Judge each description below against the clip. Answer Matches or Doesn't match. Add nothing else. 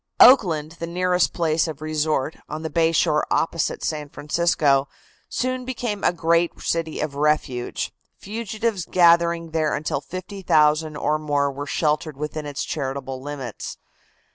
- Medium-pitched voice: Matches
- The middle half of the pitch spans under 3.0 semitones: Matches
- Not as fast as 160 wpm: Matches